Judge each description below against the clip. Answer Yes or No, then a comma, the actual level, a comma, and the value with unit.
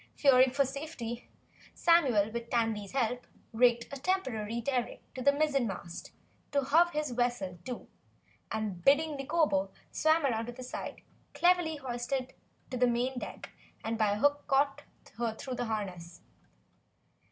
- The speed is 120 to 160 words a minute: Yes, average, 140 wpm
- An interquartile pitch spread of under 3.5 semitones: No, average, 4.0 semitones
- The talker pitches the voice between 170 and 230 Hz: No, very high, 250 Hz